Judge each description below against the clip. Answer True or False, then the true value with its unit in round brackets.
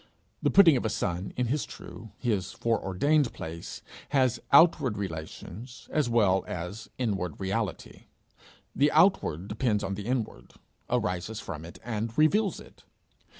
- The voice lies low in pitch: True (110 Hz)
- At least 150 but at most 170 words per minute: False (140 wpm)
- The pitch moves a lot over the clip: True (5.7 semitones)